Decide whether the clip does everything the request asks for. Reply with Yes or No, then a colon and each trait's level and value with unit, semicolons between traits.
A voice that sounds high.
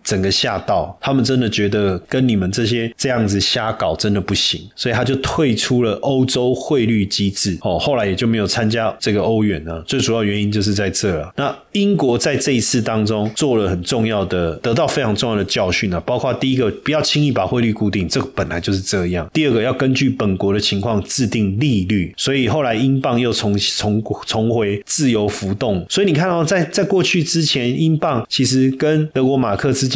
No: low, 115 Hz